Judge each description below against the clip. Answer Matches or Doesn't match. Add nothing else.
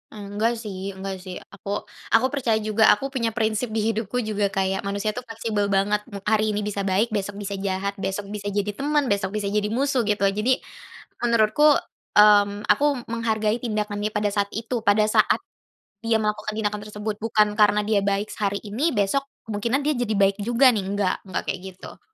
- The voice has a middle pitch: Doesn't match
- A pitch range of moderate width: Doesn't match